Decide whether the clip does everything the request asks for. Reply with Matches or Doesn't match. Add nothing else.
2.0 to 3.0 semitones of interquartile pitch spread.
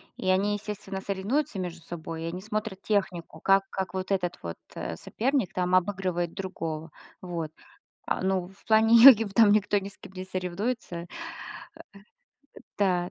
Matches